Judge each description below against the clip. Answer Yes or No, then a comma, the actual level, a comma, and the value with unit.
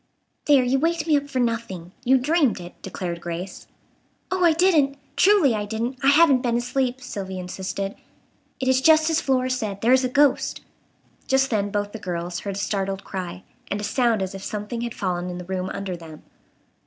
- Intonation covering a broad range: Yes, wide, 5.9 semitones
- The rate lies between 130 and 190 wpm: No, average, 200 wpm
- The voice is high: Yes, high, 230 Hz